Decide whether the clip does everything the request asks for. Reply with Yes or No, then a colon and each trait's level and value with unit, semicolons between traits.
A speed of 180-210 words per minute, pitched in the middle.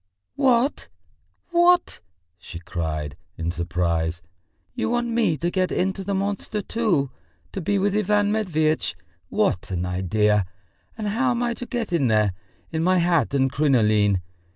No: average, 150 wpm; medium, 170 Hz